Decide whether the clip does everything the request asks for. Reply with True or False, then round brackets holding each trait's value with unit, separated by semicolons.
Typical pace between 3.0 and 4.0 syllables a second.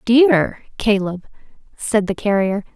True (3.7 syllables/s)